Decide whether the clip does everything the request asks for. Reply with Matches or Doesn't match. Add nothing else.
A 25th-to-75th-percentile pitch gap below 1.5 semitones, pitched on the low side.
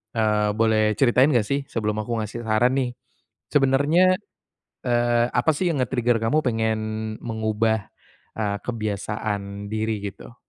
Doesn't match